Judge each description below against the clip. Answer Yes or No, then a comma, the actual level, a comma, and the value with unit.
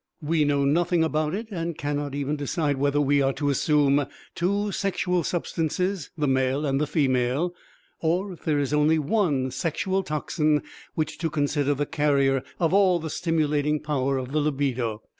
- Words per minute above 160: Yes, average, 170 wpm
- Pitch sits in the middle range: Yes, medium, 150 Hz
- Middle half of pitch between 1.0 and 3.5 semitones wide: Yes, average, 2.9 semitones